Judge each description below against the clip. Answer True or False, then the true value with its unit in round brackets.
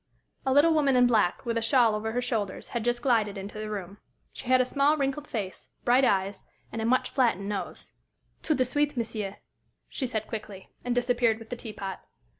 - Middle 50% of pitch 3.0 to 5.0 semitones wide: True (3.4 semitones)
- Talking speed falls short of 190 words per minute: False (205 wpm)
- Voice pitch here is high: True (230 Hz)